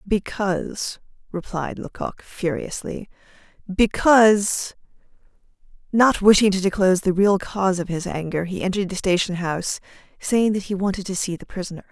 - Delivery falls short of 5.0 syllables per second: No, 5.3 syllables/s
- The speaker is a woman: Yes, female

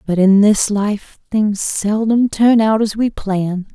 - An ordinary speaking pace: Yes, average, 175 wpm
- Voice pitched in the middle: No, high, 210 Hz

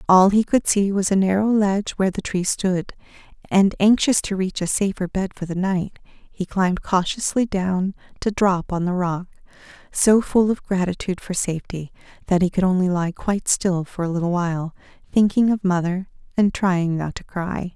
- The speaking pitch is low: No, high, 190 Hz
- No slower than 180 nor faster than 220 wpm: Yes, average, 190 wpm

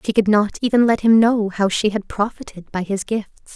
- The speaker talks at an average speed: No, fast, 235 wpm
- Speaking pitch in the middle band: No, high, 210 Hz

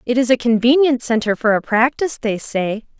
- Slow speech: No, average, 200 wpm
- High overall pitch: Yes, high, 235 Hz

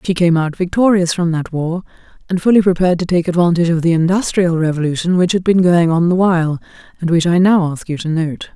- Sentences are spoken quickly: Yes, fast, 225 wpm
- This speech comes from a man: No, female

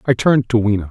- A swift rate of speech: Yes, fast, 265 wpm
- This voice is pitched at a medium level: No, low, 115 Hz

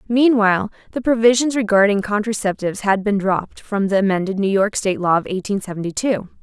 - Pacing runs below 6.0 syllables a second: No, 6.1 syllables/s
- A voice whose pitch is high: Yes, high, 205 Hz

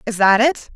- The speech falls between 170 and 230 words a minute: No, fast, 240 wpm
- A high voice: Yes, high, 230 Hz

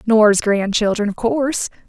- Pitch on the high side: Yes, high, 215 Hz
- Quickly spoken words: No, slow, 130 wpm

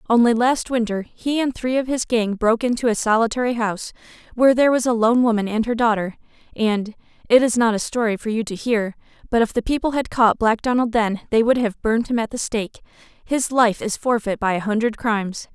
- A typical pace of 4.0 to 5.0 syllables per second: No, 5.8 syllables/s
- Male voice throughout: No, female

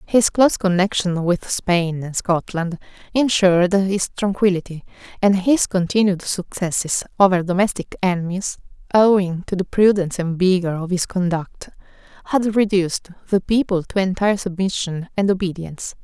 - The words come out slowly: Yes, slow, 130 wpm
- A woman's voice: Yes, female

